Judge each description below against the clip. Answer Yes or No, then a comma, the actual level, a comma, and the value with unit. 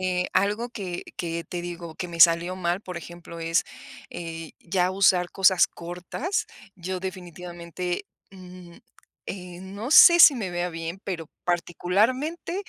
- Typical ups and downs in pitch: No, narrow, 1.9 semitones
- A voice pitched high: No, medium, 180 Hz